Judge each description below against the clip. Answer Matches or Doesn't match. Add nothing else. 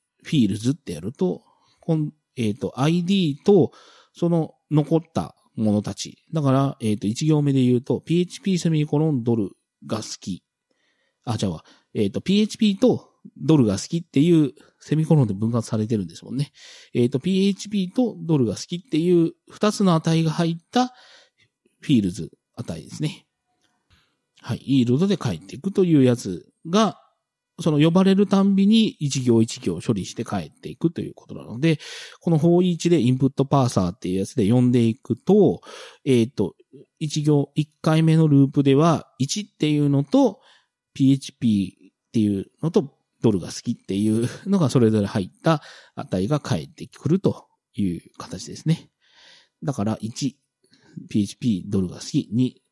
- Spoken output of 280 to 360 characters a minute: Matches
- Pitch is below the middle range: Doesn't match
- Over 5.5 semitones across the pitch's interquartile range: Matches